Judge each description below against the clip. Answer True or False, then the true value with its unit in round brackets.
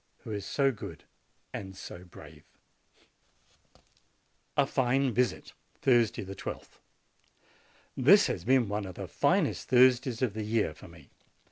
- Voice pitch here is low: True (110 Hz)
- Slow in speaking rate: True (130 wpm)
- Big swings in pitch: False (5.0 semitones)